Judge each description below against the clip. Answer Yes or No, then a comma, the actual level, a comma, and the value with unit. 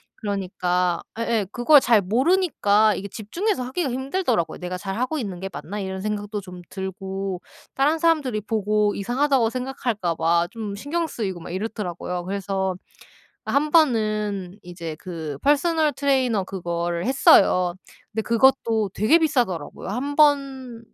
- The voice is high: Yes, high, 215 Hz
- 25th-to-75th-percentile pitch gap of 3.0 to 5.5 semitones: No, wide, 5.9 semitones